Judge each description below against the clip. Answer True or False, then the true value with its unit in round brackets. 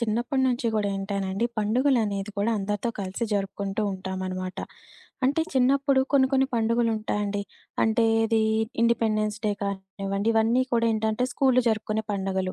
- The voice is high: True (215 Hz)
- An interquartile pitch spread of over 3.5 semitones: False (3.1 semitones)